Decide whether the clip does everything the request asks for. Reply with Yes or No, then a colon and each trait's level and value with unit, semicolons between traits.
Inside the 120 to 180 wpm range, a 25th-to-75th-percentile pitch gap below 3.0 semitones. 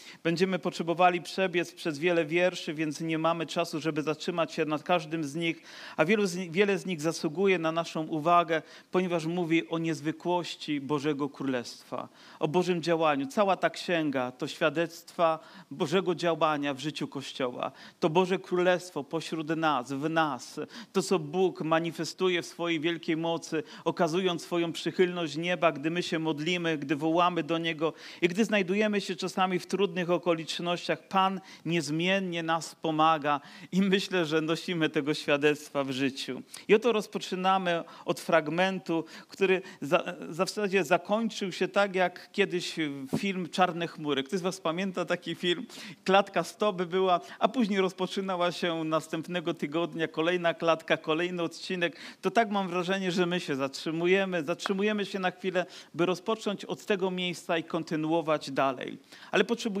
Yes: average, 155 wpm; narrow, 2.5 semitones